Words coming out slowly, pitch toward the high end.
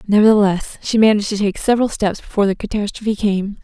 No: average, 180 wpm; high, 205 Hz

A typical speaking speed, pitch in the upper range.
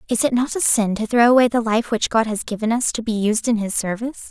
No: fast, 295 wpm; high, 230 Hz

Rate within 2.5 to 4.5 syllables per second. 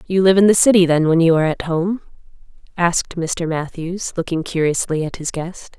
No: 5.3 syllables/s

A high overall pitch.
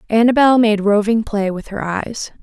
Yes: high, 215 Hz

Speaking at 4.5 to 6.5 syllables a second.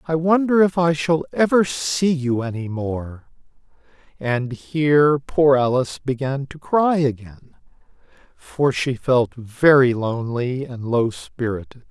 No: 3.9 syllables/s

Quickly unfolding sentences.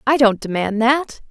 No: average, 185 wpm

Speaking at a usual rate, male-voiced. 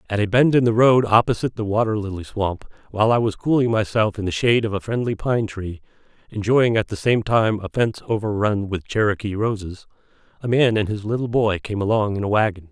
No: fast, 210 wpm; male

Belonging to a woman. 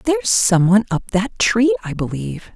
Yes: female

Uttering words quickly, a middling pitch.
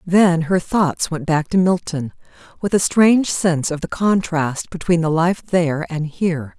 No: average, 180 wpm; medium, 170 Hz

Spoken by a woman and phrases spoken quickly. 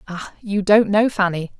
No: female; average, 190 wpm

